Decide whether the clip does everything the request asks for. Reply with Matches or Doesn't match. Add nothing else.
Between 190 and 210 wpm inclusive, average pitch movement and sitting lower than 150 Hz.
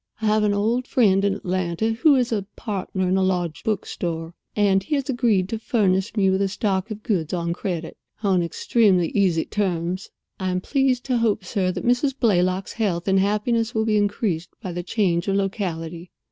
Doesn't match